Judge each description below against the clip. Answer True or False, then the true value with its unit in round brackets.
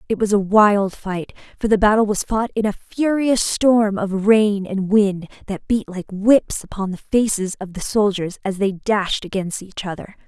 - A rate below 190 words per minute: False (200 wpm)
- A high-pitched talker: True (205 Hz)